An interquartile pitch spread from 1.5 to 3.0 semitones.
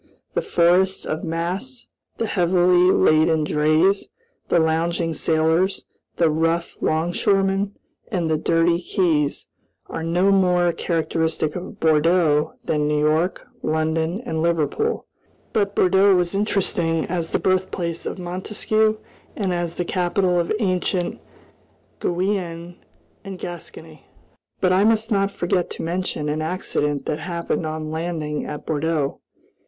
Yes: average, 2.7 semitones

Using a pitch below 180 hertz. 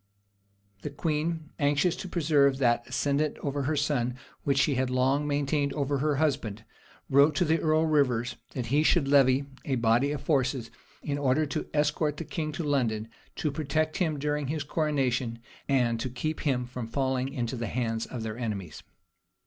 Yes: medium, 140 Hz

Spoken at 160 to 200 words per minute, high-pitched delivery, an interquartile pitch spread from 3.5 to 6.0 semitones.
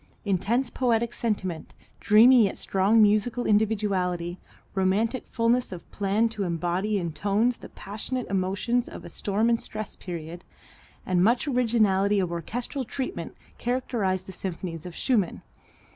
No: slow, 135 wpm; high, 205 Hz; average, 4.0 semitones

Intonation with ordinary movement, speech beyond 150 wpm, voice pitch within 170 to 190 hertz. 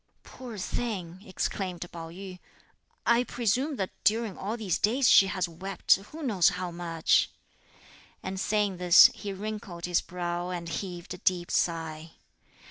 No: average, 3.3 semitones; average, 145 wpm; medium, 185 Hz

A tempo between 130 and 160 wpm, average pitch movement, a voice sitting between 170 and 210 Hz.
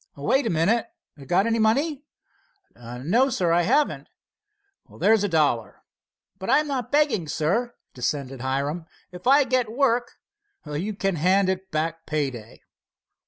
No: slow, 135 wpm; wide, 8.1 semitones; high, 190 Hz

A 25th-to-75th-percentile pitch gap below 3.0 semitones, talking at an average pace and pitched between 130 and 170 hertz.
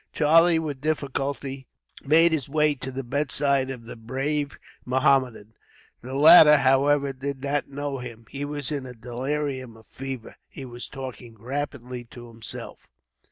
Yes: narrow, 2.5 semitones; average, 150 wpm; low, 135 Hz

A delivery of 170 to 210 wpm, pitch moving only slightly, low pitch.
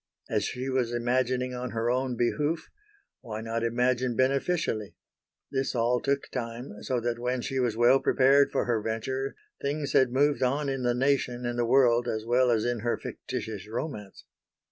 Yes: average, 175 wpm; narrow, 2.2 semitones; low, 125 Hz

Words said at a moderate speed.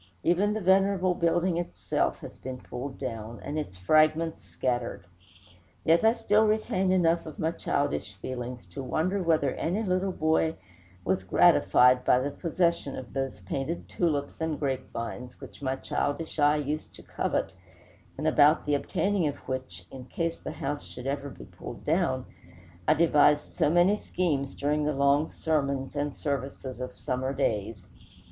Yes: average, 160 wpm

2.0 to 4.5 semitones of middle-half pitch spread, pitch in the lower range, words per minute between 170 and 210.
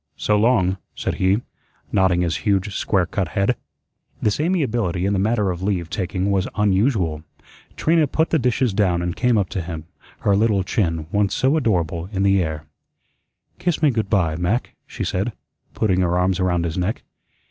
Yes: average, 3.8 semitones; very low, 95 Hz; average, 180 wpm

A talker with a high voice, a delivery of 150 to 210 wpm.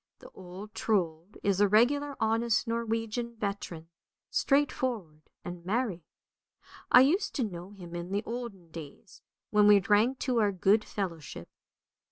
No: high, 210 Hz; average, 140 wpm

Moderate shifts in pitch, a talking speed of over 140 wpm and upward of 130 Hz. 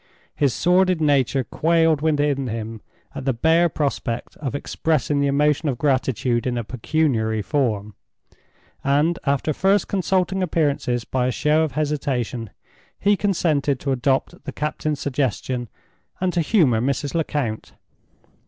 No: average, 4.2 semitones; slow, 135 wpm; medium, 140 Hz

